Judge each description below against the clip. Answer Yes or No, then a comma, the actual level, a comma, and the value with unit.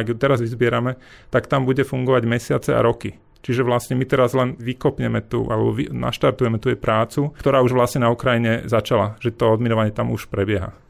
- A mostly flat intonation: Yes, narrow, 2.3 semitones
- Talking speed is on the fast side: Yes, fast, 195 wpm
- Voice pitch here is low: Yes, low, 120 Hz